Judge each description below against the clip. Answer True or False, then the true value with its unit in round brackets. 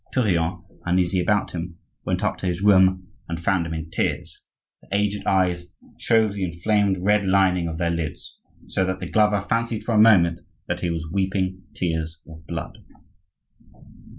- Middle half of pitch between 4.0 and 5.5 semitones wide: False (3.0 semitones)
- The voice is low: True (95 Hz)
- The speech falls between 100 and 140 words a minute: False (170 wpm)